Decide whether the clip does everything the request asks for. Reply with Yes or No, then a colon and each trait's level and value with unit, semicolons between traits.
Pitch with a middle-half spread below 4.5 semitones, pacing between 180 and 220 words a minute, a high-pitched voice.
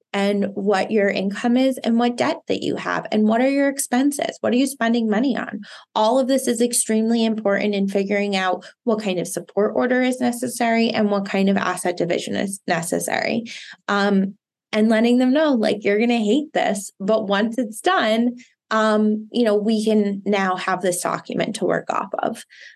Yes: average, 3.2 semitones; average, 195 wpm; high, 220 Hz